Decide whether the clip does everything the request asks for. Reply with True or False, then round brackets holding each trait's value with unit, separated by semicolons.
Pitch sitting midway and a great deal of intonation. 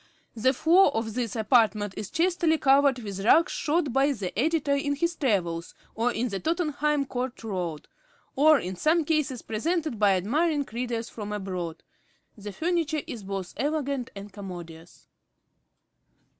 False (245 Hz; 6.7 semitones)